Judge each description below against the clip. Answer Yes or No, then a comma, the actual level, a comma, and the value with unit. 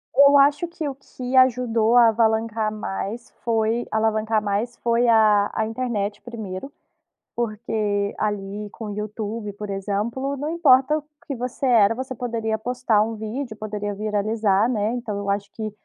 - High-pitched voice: Yes, high, 220 Hz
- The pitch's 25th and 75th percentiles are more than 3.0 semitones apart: No, average, 2.7 semitones